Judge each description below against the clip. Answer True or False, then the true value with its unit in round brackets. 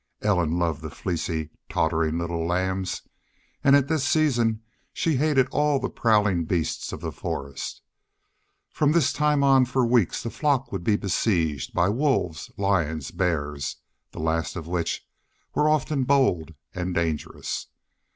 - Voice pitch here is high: False (95 Hz)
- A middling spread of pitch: False (8.4 semitones)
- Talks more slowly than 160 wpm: True (145 wpm)